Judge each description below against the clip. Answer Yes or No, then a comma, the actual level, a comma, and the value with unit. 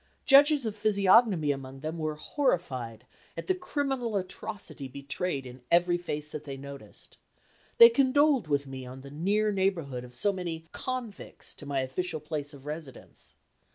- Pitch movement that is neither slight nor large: No, wide, 7.4 semitones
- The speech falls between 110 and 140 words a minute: No, average, 155 wpm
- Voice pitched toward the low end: No, medium, 165 Hz